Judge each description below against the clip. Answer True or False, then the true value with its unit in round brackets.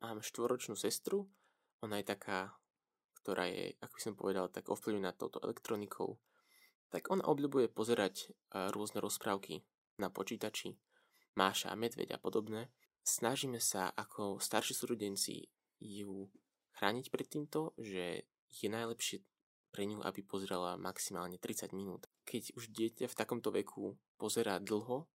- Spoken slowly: False (130 wpm)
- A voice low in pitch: True (105 Hz)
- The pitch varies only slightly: False (3.5 semitones)